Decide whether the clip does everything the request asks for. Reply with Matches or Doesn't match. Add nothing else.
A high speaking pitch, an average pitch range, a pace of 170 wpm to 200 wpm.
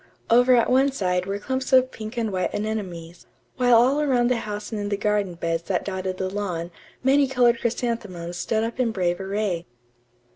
Matches